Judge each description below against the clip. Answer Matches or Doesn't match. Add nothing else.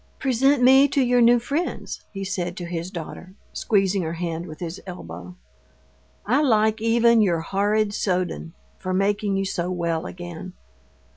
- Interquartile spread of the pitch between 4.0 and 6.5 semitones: Matches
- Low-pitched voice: Doesn't match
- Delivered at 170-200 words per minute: Doesn't match